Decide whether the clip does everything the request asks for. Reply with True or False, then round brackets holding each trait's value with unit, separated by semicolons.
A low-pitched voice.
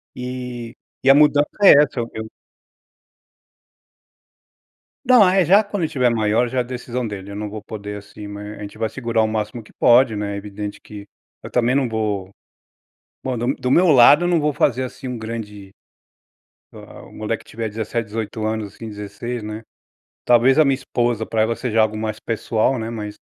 True (115 Hz)